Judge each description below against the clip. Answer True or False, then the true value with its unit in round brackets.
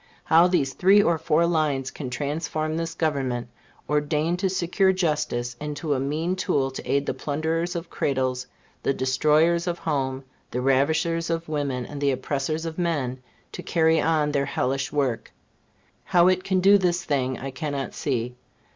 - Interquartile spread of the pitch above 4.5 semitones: False (3.7 semitones)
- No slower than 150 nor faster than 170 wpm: True (165 wpm)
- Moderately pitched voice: True (150 Hz)